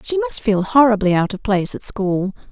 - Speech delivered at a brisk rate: Yes, fast, 215 wpm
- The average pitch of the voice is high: Yes, high, 220 Hz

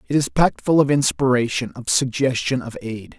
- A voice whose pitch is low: Yes, low, 130 Hz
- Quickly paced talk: No, average, 190 wpm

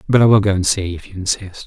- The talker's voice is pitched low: Yes, low, 100 Hz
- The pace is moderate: No, fast, 325 wpm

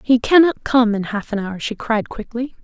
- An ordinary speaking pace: No, fast, 225 wpm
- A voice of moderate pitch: No, high, 235 Hz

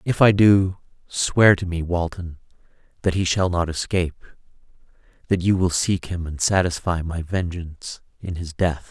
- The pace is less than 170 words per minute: Yes, average, 160 wpm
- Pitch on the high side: No, very low, 90 Hz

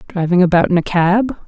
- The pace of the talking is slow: No, fast, 205 wpm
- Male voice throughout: No, female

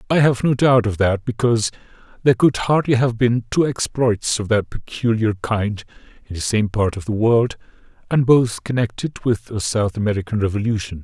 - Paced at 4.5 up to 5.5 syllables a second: Yes, 5.2 syllables/s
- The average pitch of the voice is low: Yes, low, 110 Hz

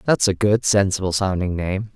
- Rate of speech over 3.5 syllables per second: Yes, 5.0 syllables/s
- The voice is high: No, low, 100 Hz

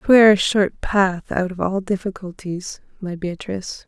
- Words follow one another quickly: No, average, 155 wpm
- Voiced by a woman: Yes, female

